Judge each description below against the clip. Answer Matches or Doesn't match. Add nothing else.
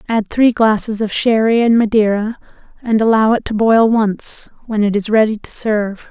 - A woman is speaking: Matches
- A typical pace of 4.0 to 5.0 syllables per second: Matches